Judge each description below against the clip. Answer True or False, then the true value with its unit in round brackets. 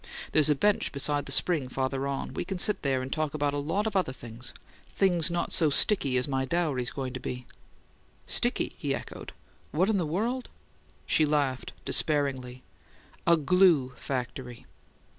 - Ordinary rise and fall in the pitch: True (4.8 semitones)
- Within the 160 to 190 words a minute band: True (170 wpm)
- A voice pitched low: False (145 Hz)